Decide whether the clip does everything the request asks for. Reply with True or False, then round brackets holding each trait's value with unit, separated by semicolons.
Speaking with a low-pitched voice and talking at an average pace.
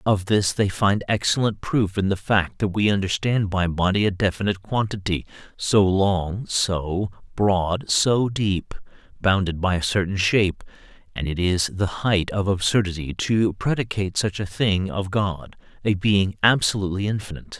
True (100 Hz; 155 wpm)